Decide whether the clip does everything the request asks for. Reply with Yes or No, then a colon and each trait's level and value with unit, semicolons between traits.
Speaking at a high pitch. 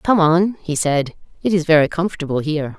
No: medium, 160 Hz